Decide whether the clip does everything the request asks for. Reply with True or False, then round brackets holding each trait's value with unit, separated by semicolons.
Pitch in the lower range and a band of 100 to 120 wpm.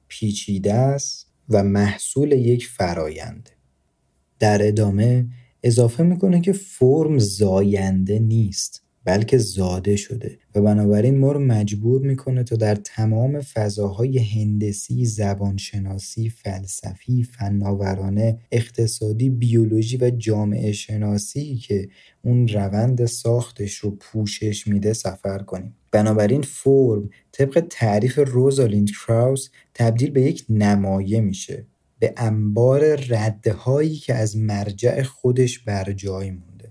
True (110 Hz; 110 wpm)